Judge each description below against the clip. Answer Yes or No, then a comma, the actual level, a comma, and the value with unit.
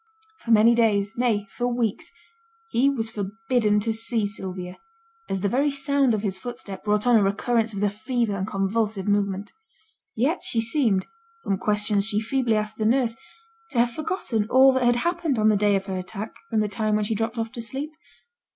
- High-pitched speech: Yes, high, 220 Hz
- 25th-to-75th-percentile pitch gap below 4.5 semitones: Yes, average, 2.9 semitones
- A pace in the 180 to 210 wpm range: Yes, average, 195 wpm